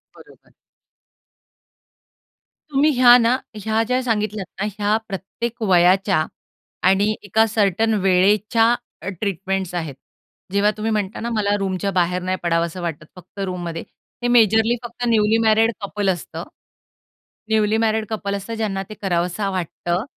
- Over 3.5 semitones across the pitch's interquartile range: No, average, 3.1 semitones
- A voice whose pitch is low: No, high, 200 Hz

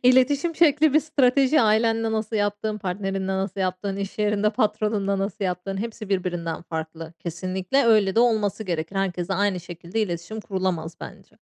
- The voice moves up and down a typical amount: Yes, average, 3.3 semitones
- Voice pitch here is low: No, high, 200 Hz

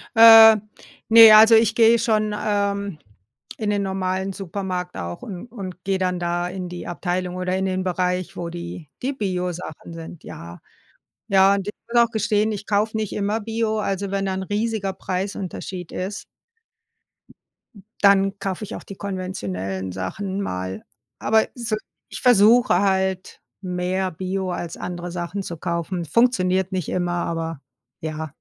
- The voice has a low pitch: No, high, 190 Hz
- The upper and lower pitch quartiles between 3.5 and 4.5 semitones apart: No, average, 2.8 semitones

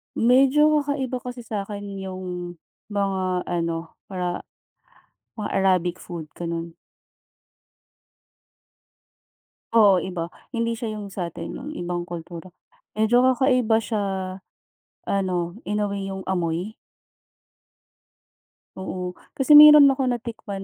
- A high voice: Yes, high, 195 Hz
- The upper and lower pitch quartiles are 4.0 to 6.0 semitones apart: Yes, average, 4.7 semitones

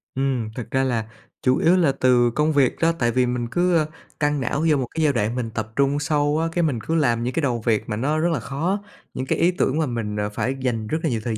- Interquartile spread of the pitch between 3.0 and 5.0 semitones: Yes, average, 4.5 semitones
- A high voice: No, low, 130 Hz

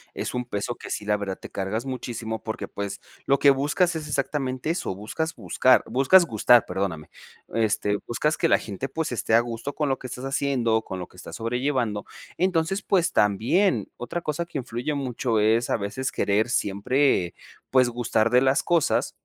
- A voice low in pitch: Yes, low, 125 Hz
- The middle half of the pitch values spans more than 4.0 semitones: Yes, average, 4.7 semitones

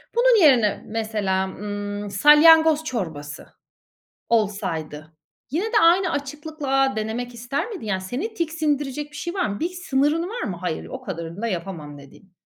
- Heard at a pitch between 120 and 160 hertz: No, high, 245 Hz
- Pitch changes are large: Yes, wide, 8.3 semitones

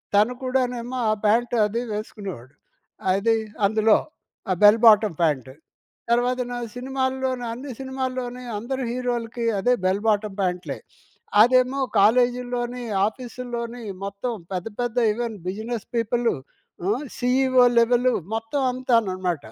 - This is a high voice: Yes, high, 240 Hz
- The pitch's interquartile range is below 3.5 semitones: Yes, average, 2.9 semitones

